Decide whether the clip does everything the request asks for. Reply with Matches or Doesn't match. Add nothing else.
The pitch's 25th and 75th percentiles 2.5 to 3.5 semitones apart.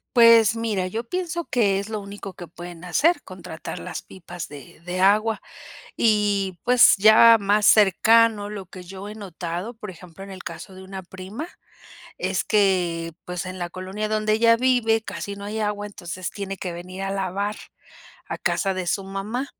Matches